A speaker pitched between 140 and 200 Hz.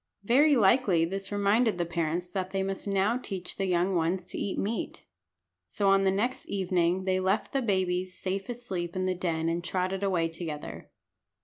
Yes: high, 190 Hz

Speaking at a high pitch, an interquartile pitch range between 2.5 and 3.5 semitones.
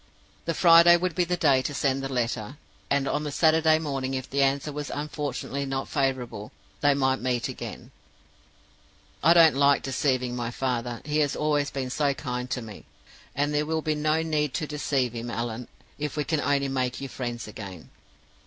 No: medium, 140 Hz; average, 2.9 semitones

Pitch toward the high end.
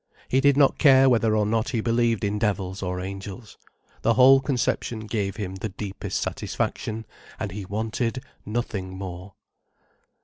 No: low, 110 Hz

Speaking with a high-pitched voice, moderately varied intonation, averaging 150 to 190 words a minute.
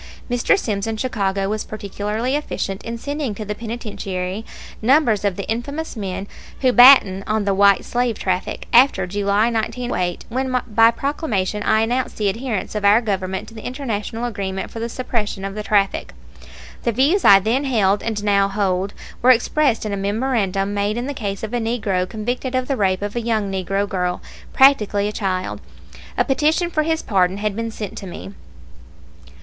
Yes: high, 215 Hz; average, 3.7 semitones; average, 180 wpm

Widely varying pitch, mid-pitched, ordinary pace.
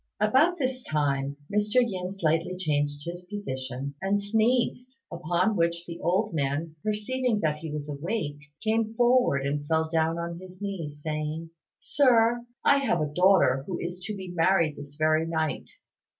Yes: wide, 5.7 semitones; medium, 170 Hz; average, 160 wpm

